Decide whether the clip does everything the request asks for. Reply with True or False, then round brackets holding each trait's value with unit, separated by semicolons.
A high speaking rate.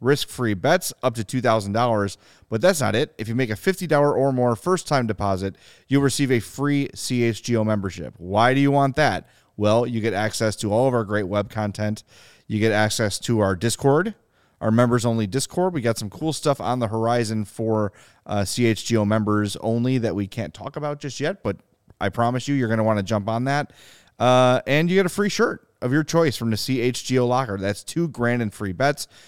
True (215 wpm)